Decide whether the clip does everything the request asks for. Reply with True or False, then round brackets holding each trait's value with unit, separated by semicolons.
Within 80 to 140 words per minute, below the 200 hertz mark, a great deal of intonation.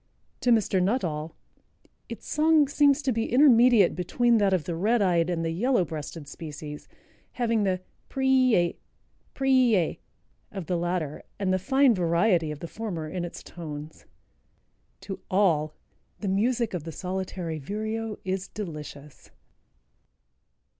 True (135 wpm; 190 Hz; 5.8 semitones)